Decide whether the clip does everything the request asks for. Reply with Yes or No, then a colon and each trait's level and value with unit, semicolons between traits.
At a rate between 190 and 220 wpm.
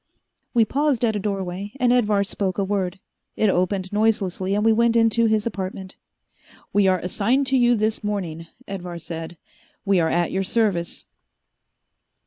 No: average, 160 wpm